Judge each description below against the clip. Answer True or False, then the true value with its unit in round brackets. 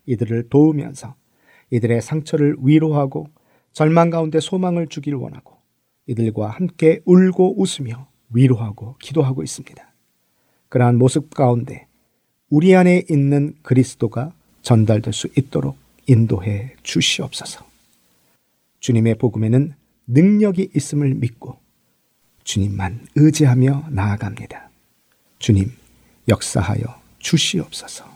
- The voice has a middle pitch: False (130 Hz)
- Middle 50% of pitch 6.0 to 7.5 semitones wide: False (5.1 semitones)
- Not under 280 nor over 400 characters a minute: False (265 characters per minute)